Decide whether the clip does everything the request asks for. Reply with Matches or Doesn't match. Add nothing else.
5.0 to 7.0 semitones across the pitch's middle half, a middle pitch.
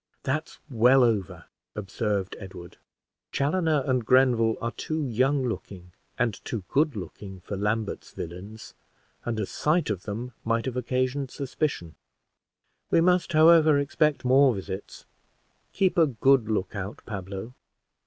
Doesn't match